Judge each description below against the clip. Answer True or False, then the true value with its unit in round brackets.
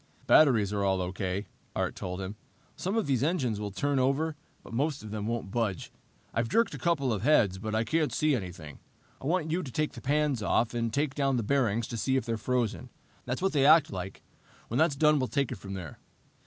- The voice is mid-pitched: False (125 Hz)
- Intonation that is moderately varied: False (6.2 semitones)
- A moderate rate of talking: False (225 wpm)